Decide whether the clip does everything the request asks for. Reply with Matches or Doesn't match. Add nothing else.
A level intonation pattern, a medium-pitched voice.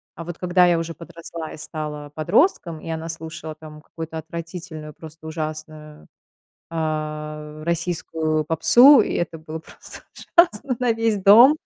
Matches